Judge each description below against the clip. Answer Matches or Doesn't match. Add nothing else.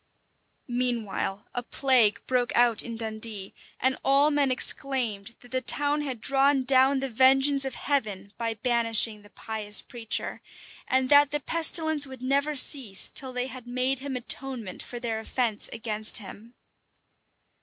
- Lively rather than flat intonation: Doesn't match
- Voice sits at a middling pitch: Doesn't match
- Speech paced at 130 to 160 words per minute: Matches